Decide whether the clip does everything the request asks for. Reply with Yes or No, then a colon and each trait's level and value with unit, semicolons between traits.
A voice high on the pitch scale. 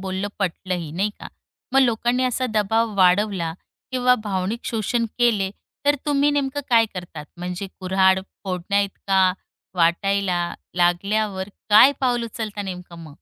Yes: high, 200 Hz